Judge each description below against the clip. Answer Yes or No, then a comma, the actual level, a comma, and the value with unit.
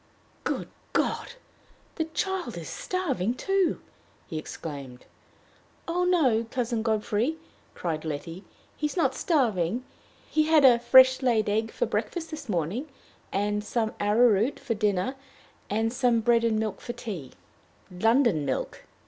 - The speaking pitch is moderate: No, high, 230 Hz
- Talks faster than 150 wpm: No, average, 140 wpm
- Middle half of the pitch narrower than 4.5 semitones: No, average, 5.0 semitones